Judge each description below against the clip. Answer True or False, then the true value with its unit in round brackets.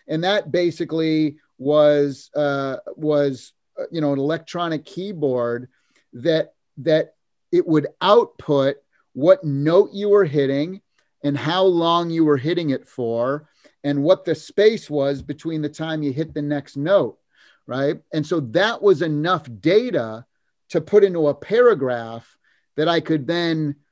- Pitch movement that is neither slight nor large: True (3.2 semitones)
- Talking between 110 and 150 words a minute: True (145 wpm)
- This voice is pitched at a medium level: True (155 Hz)